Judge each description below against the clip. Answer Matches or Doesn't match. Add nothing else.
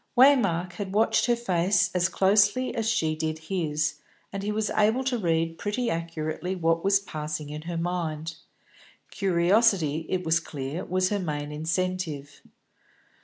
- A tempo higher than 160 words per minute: Doesn't match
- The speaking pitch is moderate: Matches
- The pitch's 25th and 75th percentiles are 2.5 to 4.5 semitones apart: Matches